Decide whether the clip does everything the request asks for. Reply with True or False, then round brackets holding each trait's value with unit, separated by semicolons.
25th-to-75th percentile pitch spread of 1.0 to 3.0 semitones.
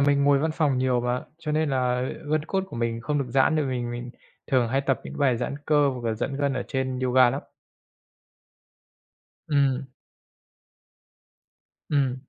True (2.4 semitones)